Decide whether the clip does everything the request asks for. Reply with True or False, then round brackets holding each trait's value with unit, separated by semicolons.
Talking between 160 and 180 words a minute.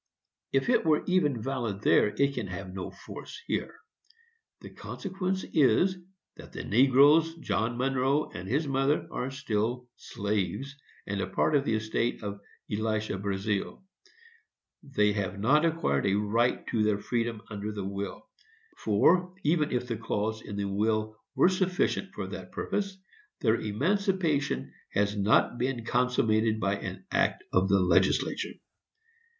False (145 wpm)